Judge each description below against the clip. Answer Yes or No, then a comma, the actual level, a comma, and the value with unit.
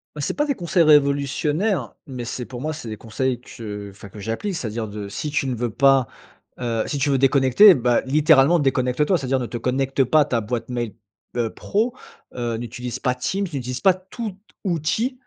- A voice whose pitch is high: No, low, 135 Hz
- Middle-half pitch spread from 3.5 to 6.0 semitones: Yes, average, 4.5 semitones